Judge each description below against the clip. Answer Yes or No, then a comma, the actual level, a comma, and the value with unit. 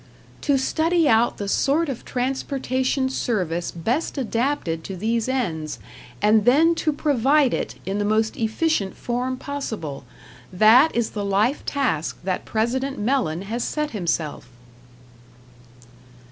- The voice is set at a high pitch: Yes, high, 240 Hz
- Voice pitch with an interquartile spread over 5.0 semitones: Yes, wide, 5.4 semitones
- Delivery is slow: Yes, slow, 130 wpm